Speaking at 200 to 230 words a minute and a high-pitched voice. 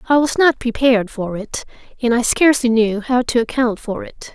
Yes: fast, 205 wpm; high, 240 Hz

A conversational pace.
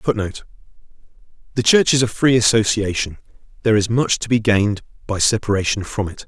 Yes: average, 160 wpm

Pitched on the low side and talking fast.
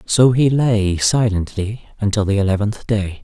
No: low, 105 Hz; average, 150 wpm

